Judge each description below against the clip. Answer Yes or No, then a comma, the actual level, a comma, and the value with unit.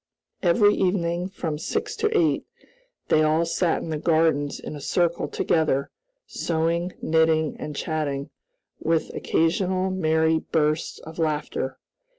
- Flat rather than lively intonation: Yes, narrow, 2.1 semitones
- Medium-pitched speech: Yes, medium, 160 Hz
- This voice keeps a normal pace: No, slow, 130 wpm